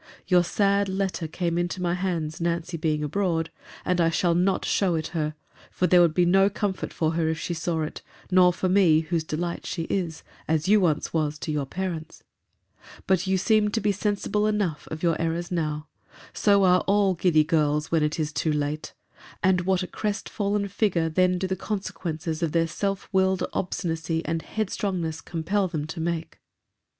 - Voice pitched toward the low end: No, medium, 175 Hz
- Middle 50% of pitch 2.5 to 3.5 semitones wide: Yes, average, 3.0 semitones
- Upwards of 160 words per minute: Yes, average, 185 wpm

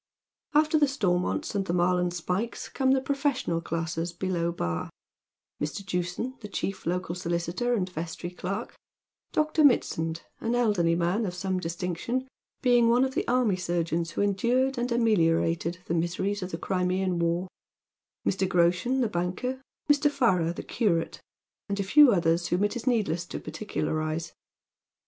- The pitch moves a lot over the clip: Yes, wide, 5.8 semitones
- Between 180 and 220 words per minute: No, average, 160 wpm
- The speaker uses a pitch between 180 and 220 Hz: Yes, medium, 185 Hz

